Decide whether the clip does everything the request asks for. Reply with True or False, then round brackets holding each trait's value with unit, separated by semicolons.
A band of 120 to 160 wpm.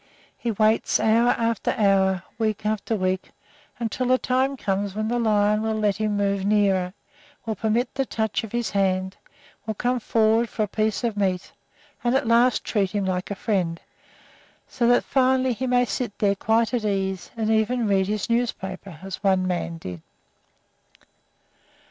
False (170 wpm)